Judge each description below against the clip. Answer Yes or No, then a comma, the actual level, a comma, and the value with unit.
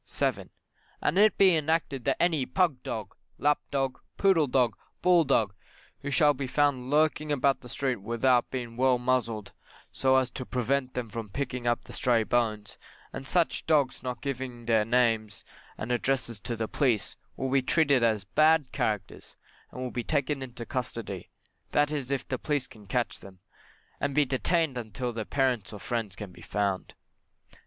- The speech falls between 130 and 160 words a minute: No, average, 175 wpm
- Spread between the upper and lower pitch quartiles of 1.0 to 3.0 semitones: No, average, 3.5 semitones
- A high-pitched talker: No, low, 125 Hz